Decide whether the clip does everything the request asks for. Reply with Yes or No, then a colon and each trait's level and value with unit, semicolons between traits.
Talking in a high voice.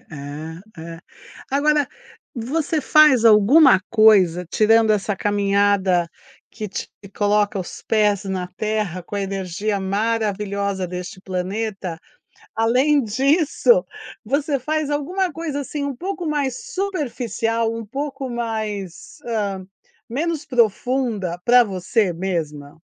Yes: high, 215 Hz